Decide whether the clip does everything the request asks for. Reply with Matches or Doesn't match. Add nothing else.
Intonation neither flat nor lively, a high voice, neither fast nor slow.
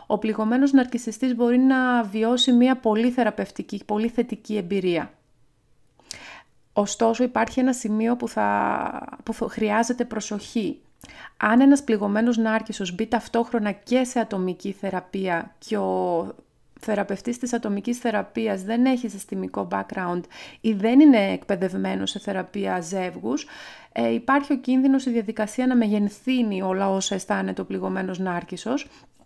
Matches